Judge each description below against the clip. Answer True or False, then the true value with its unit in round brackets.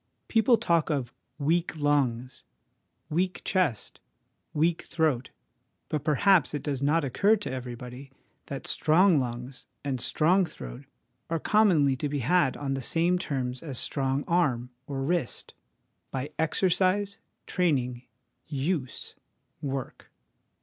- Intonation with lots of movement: False (4.6 semitones)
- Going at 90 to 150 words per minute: True (135 wpm)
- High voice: False (145 Hz)